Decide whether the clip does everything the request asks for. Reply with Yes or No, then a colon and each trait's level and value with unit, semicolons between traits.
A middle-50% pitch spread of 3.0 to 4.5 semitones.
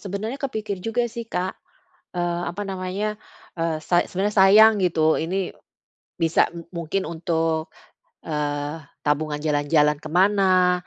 Yes: average, 3.9 semitones